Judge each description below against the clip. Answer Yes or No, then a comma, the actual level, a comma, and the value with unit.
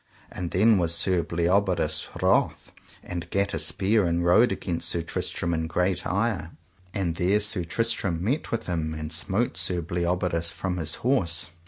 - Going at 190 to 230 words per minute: No, average, 165 wpm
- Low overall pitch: Yes, very low, 90 Hz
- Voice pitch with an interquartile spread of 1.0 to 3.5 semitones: Yes, average, 2.9 semitones